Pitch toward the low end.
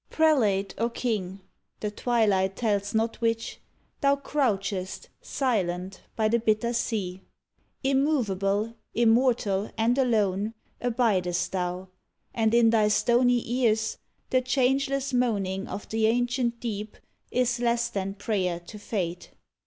No: high, 225 Hz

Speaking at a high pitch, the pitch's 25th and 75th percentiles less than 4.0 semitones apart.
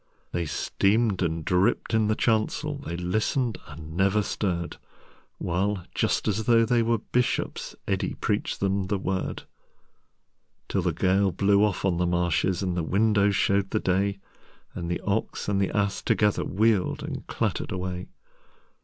No: low, 100 Hz; average, 3.0 semitones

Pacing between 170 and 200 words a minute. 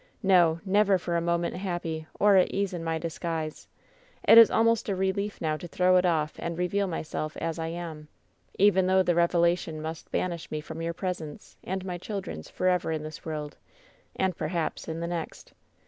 Yes: average, 195 wpm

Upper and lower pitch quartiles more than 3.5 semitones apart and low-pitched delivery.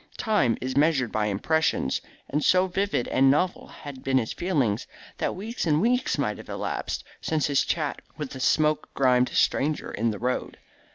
No: average, 4.6 semitones; medium, 145 Hz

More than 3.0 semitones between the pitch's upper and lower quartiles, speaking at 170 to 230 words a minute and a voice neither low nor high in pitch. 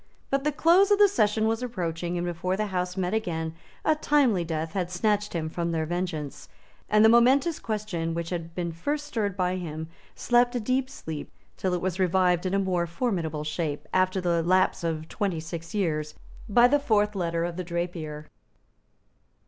Yes: average, 4.6 semitones; average, 190 wpm; medium, 180 Hz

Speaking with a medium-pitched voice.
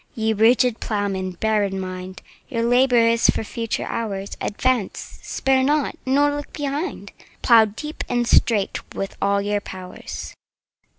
No: high, 225 Hz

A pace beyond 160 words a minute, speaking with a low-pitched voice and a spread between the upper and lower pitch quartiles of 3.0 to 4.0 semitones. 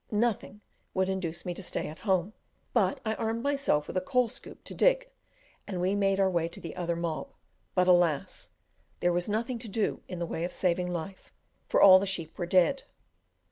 No: fast, 205 wpm; medium, 185 Hz; average, 3.7 semitones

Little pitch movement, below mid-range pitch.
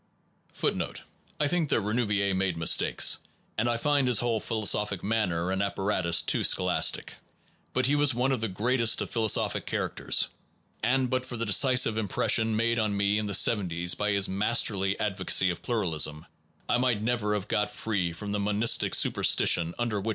No: average, 3.5 semitones; low, 105 Hz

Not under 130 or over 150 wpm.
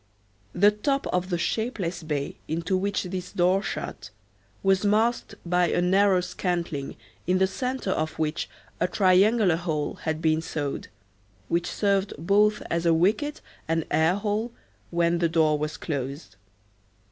Yes: average, 145 wpm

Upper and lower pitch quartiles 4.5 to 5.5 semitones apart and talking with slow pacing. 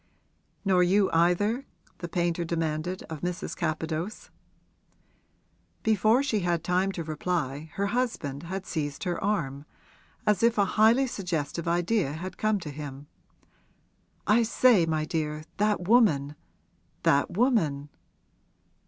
Yes: average, 5.1 semitones; slow, 125 wpm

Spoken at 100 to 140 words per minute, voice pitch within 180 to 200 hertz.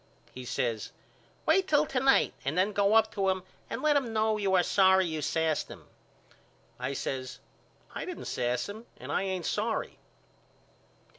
No: average, 170 wpm; high, 190 Hz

